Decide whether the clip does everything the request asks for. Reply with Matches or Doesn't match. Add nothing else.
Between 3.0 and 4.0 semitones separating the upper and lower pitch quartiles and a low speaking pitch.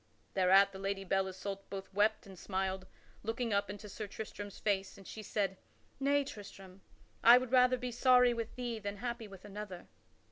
Doesn't match